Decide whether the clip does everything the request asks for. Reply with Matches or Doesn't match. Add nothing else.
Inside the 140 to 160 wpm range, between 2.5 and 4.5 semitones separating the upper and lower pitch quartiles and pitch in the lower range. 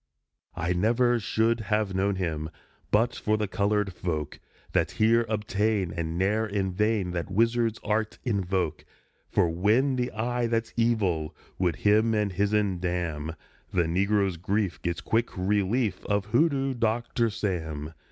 Matches